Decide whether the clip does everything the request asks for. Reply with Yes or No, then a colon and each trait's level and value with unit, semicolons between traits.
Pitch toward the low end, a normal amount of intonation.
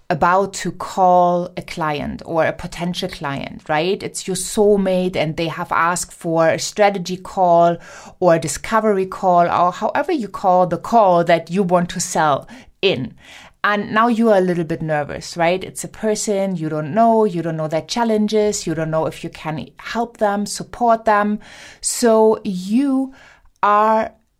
No: medium, 185 Hz; average, 3.8 semitones